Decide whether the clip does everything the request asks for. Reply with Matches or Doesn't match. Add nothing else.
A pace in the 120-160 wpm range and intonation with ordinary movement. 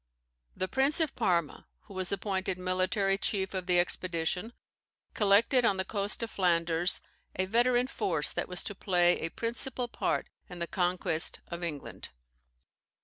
Matches